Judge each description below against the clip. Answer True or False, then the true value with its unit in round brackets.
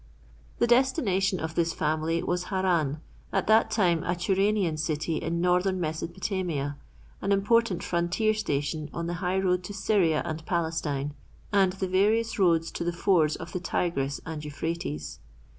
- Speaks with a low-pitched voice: False (175 Hz)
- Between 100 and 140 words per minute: False (155 wpm)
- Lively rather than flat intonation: False (3.3 semitones)